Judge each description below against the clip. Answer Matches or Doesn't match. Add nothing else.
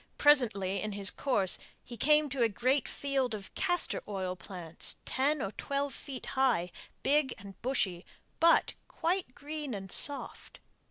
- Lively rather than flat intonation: Matches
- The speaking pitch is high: Matches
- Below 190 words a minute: Matches